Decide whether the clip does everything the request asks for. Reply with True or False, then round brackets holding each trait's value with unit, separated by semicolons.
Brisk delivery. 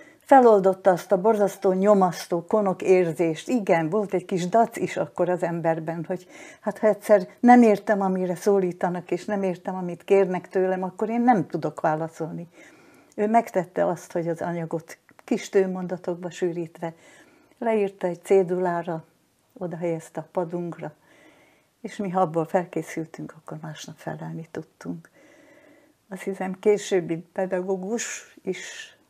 False (130 wpm)